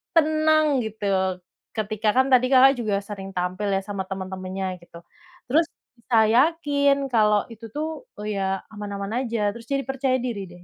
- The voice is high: Yes, high, 215 Hz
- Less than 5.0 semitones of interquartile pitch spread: No, wide, 5.6 semitones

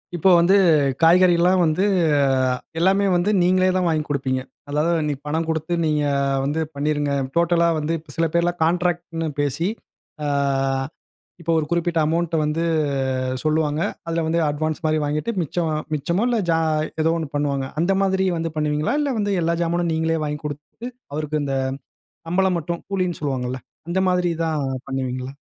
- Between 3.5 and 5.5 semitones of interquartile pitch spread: No, average, 2.7 semitones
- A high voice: No, medium, 165 Hz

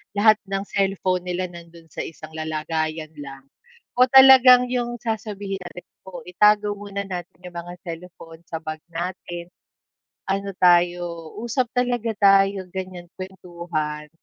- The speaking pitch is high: No, medium, 180 Hz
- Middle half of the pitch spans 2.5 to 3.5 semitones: Yes, average, 3.2 semitones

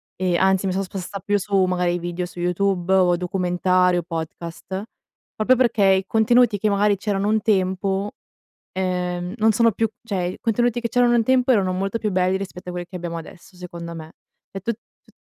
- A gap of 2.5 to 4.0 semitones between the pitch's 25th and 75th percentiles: Yes, average, 2.8 semitones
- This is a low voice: No, high, 190 Hz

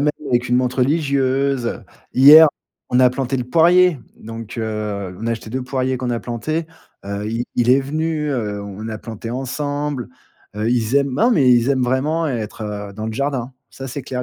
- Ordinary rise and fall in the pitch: Yes, average, 3.5 semitones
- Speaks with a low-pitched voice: Yes, low, 125 Hz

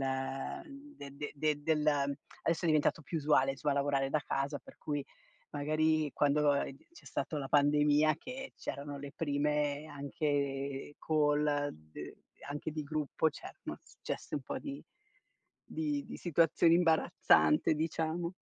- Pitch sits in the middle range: Yes, medium, 150 Hz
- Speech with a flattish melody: Yes, narrow, 2.0 semitones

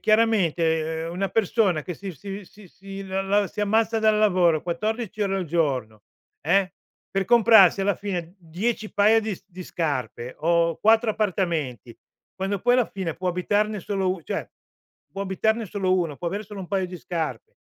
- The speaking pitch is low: No, high, 190 Hz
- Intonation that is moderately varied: Yes, average, 3.7 semitones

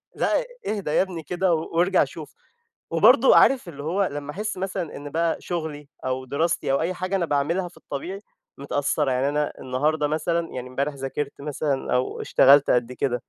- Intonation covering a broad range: No, average, 3.9 semitones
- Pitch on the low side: No, medium, 150 Hz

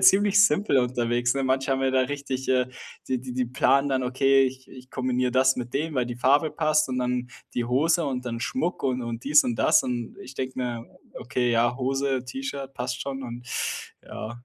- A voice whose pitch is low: Yes, low, 130 Hz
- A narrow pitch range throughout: Yes, narrow, 1.7 semitones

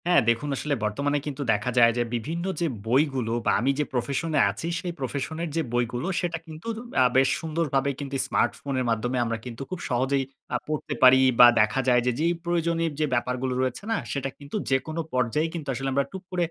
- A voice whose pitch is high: No, low, 135 Hz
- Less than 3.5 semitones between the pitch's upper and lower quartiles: No, average, 4.3 semitones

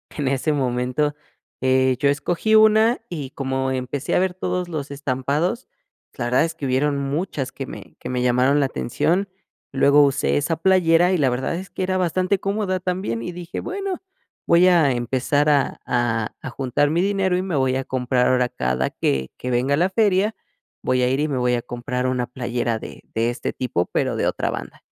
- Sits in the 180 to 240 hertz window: No, medium, 140 Hz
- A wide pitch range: Yes, wide, 6.0 semitones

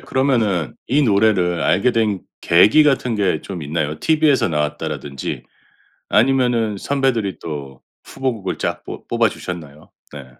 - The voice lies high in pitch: No, low, 100 Hz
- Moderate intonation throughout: No, wide, 8.0 semitones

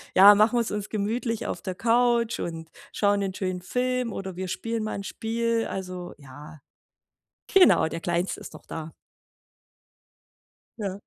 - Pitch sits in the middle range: No, high, 200 Hz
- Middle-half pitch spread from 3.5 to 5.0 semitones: Yes, average, 4.1 semitones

